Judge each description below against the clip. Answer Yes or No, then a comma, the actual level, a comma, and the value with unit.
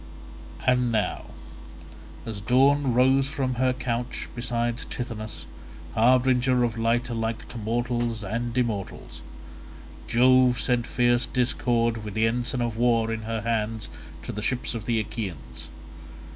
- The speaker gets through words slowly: Yes, slow, 130 wpm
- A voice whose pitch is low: Yes, low, 120 Hz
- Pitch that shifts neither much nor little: No, narrow, 1.8 semitones